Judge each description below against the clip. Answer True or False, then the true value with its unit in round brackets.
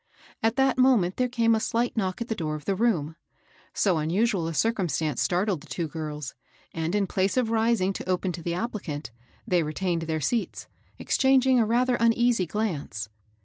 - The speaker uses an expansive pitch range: True (6.0 semitones)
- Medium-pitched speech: False (195 Hz)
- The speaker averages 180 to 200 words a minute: True (185 wpm)